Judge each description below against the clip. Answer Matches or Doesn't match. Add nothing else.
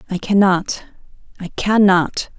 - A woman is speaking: Matches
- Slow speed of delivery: Matches